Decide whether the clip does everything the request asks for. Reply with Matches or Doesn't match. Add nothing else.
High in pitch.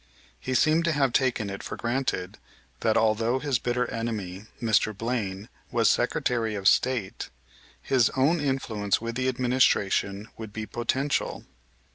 Doesn't match